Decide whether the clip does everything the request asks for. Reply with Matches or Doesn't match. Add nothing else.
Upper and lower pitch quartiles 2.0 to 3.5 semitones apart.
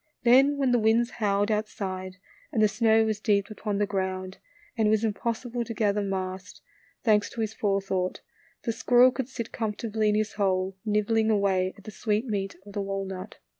Matches